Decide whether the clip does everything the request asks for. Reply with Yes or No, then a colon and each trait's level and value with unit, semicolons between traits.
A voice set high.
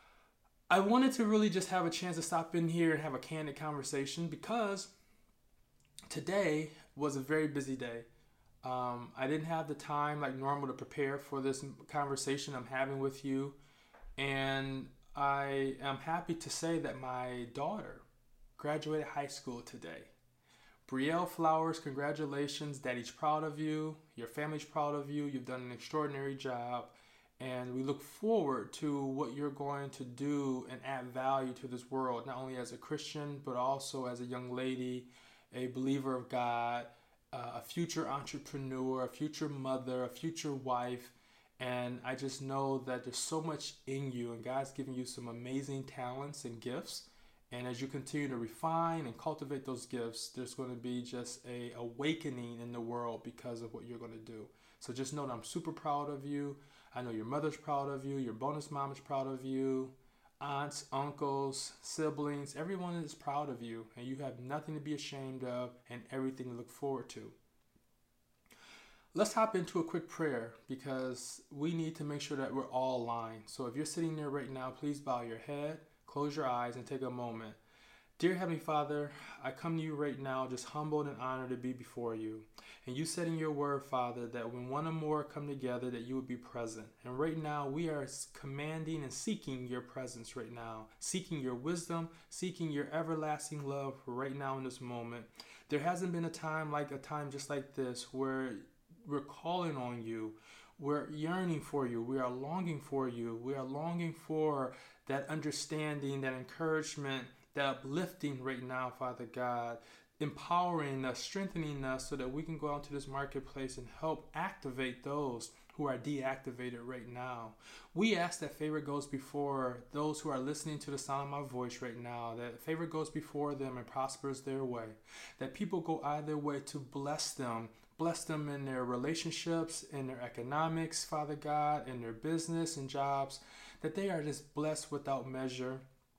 No: medium, 140 Hz